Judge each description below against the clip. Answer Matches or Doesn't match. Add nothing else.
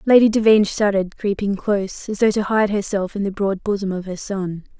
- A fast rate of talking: Matches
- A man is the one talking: Doesn't match